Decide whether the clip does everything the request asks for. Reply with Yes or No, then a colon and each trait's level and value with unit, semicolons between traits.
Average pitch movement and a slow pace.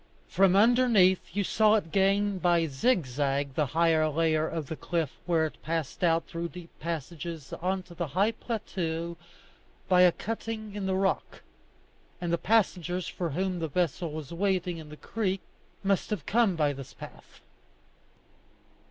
No: average, 3.3 semitones; average, 160 wpm